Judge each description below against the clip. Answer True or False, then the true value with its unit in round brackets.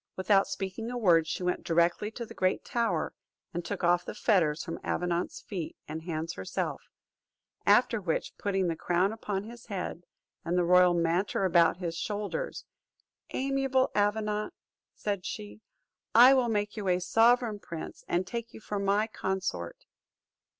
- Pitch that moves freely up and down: False (3.9 semitones)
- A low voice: False (195 Hz)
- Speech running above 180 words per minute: False (155 wpm)